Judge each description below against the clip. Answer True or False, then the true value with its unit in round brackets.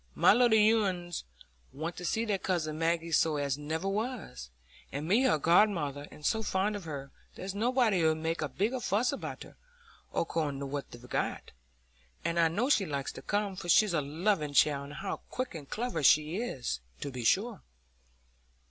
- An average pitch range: False (5.9 semitones)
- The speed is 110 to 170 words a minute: False (185 wpm)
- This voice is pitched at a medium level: True (170 Hz)